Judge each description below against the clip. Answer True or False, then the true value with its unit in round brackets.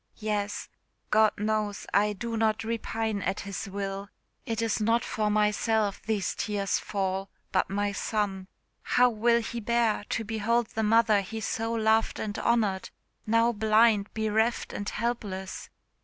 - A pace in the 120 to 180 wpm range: True (145 wpm)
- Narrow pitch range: True (1.9 semitones)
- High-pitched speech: True (215 Hz)